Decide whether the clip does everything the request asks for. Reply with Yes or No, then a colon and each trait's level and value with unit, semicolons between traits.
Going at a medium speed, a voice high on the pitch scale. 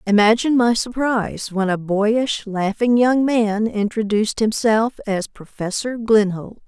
No: slow, 125 wpm; high, 220 Hz